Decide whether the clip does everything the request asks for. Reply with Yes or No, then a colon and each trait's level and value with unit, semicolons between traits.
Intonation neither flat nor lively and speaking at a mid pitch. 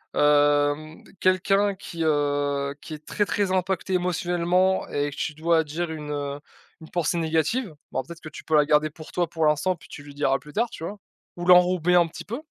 Yes: average, 3.4 semitones; medium, 160 Hz